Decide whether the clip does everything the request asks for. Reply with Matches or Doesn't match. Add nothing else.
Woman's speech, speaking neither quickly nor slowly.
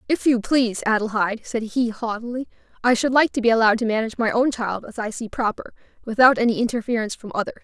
Doesn't match